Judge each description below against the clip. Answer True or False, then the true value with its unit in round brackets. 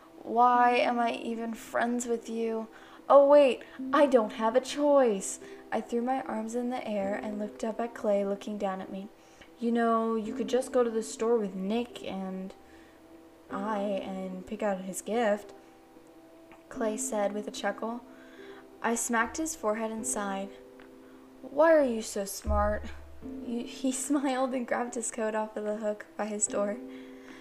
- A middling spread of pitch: True (3.6 semitones)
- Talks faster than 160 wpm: True (170 wpm)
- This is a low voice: False (220 Hz)